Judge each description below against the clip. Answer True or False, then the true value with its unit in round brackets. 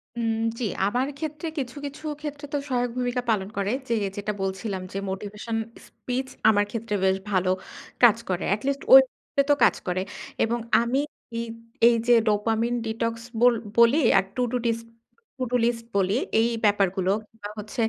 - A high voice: True (230 Hz)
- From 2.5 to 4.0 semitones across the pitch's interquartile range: True (3.3 semitones)